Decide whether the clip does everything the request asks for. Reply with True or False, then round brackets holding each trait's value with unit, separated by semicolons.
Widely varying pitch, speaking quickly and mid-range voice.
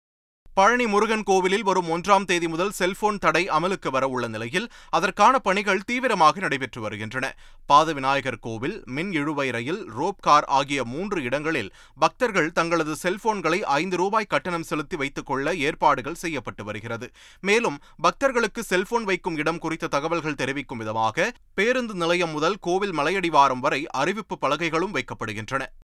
True (6.1 semitones; 135 wpm; 165 Hz)